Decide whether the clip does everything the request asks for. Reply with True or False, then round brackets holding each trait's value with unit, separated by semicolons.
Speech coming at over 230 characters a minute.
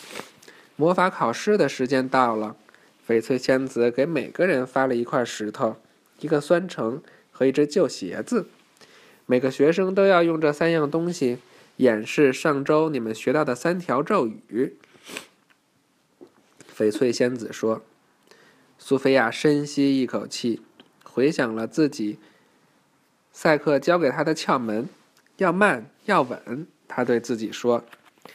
False (195 characters per minute)